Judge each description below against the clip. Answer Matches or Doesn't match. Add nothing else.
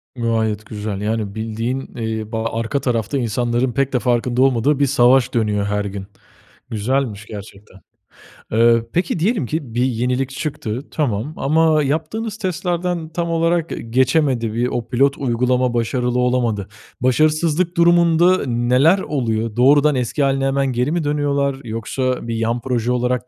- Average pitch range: Matches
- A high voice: Doesn't match